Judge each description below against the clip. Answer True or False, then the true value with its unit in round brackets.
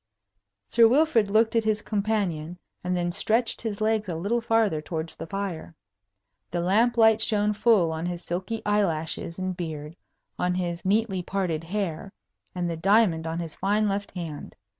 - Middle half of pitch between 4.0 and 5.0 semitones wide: True (4.3 semitones)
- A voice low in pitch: False (190 Hz)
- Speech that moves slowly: False (165 wpm)